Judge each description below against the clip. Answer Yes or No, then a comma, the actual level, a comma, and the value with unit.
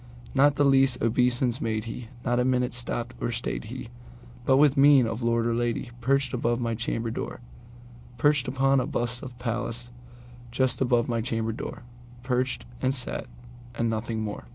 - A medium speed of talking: Yes, average, 160 wpm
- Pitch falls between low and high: No, low, 120 Hz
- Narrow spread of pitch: Yes, narrow, 1.8 semitones